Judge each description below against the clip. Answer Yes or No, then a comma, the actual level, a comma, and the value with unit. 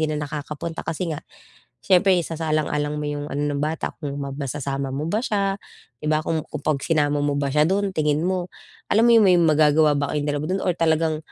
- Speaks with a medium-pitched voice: Yes, medium, 155 Hz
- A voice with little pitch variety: Yes, narrow, 2.3 semitones